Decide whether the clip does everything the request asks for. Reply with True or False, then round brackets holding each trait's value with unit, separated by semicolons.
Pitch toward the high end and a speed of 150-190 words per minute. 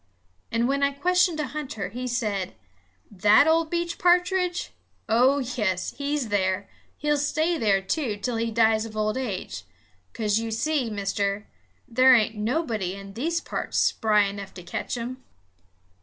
True (230 Hz; 155 wpm)